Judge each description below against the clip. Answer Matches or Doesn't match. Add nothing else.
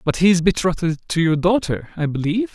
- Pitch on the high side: Doesn't match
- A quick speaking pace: Matches